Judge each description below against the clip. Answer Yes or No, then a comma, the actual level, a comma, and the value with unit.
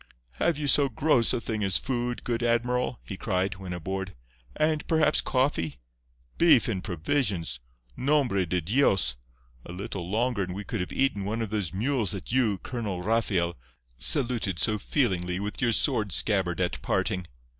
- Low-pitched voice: Yes, low, 105 Hz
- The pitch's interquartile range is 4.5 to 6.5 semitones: Yes, average, 5.1 semitones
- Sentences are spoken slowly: No, average, 165 wpm